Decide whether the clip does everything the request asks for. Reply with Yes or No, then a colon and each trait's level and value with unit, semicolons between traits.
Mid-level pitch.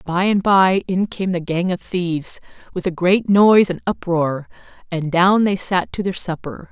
Yes: medium, 180 Hz